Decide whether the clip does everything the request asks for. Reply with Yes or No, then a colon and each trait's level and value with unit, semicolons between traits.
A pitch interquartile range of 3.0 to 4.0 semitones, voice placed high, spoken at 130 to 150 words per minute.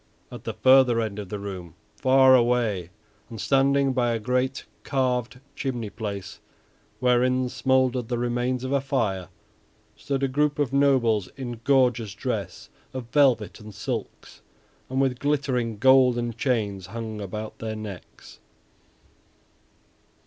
No: average, 3.3 semitones; low, 125 Hz; slow, 135 wpm